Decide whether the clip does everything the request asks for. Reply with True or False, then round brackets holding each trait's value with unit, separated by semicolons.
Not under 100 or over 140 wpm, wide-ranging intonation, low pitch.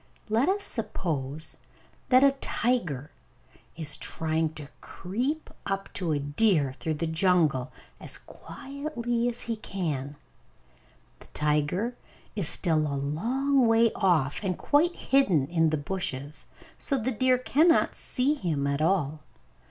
False (135 wpm; 8.4 semitones; 180 Hz)